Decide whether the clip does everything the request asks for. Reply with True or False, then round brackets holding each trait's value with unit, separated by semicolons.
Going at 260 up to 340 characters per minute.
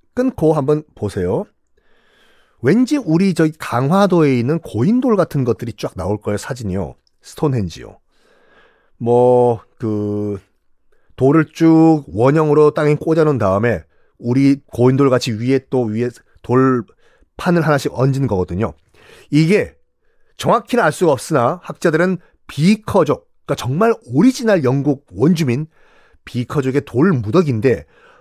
True (270 characters per minute)